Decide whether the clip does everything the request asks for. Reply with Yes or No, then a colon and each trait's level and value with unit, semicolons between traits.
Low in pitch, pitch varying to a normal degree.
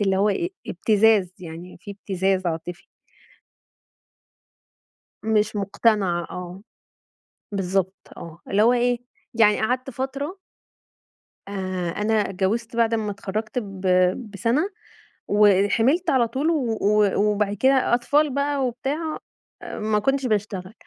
No: high, 210 Hz; average, 4.2 semitones